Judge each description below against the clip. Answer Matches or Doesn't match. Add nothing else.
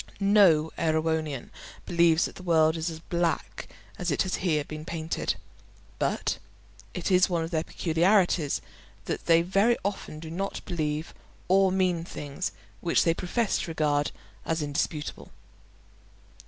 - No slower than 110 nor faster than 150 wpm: Matches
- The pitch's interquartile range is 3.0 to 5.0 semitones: Doesn't match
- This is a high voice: Doesn't match